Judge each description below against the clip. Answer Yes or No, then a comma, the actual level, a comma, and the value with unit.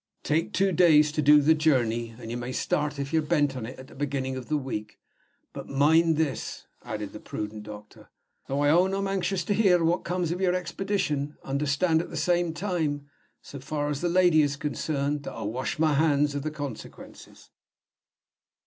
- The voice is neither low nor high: Yes, medium, 150 Hz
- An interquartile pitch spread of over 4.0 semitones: No, average, 3.7 semitones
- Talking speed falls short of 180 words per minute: No, average, 195 wpm